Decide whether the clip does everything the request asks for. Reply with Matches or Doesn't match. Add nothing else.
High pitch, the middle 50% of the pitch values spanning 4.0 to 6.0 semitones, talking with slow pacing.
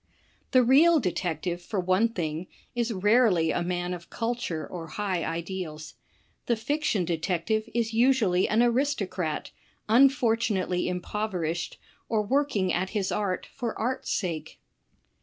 Matches